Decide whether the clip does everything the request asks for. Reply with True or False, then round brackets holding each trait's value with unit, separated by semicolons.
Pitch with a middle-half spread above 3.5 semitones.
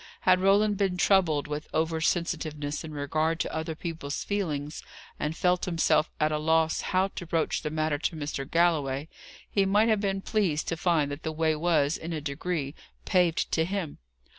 False (3.1 semitones)